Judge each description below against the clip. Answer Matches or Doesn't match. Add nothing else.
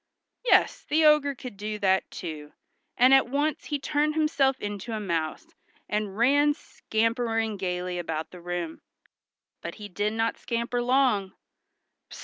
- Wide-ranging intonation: Matches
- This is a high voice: Matches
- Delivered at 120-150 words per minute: Matches